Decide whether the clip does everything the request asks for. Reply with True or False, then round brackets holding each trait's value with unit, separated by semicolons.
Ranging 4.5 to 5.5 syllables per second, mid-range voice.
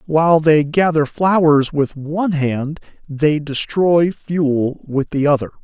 False (3.7 syllables/s; 155 Hz)